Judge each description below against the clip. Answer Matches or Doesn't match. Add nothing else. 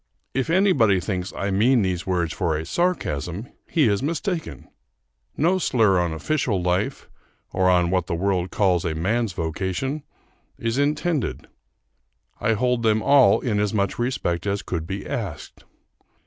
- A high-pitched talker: Doesn't match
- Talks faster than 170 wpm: Doesn't match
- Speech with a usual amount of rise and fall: Doesn't match